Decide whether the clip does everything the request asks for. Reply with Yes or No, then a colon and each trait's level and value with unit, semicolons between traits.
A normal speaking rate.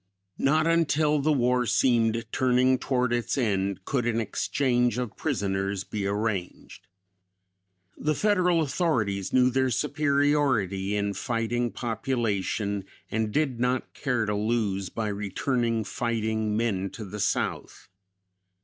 No: slow, 120 wpm